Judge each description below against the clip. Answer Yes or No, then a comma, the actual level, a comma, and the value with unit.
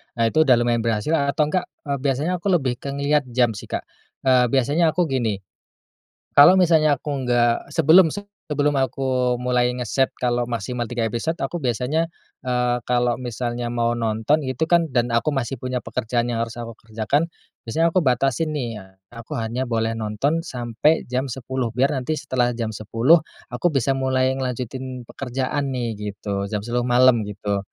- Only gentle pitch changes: No, average, 3.1 semitones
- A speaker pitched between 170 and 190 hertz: No, low, 125 Hz